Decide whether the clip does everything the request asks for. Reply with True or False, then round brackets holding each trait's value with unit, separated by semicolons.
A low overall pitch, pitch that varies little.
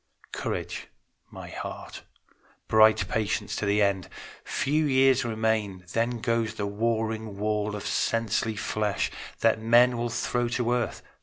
True (110 Hz; 2.0 semitones)